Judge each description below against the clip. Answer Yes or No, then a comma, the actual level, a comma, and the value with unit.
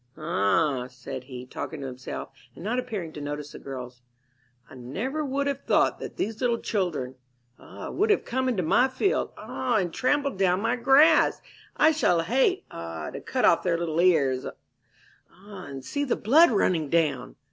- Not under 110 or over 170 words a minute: No, average, 180 wpm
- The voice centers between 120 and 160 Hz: No, medium, 180 Hz